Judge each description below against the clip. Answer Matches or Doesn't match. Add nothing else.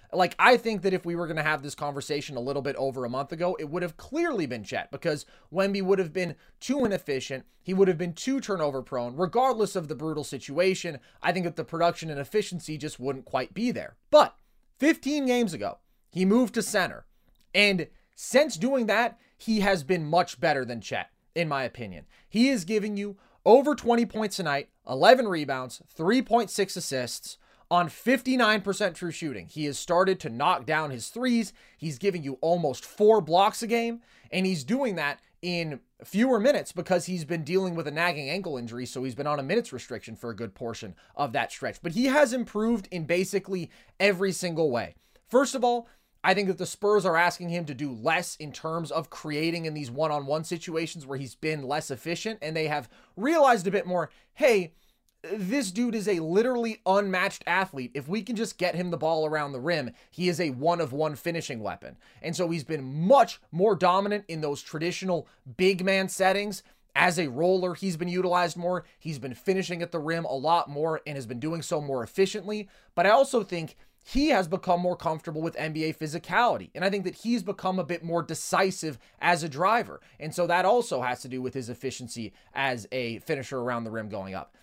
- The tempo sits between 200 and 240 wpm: Matches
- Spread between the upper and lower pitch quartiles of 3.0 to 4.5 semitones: Doesn't match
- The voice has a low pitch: Doesn't match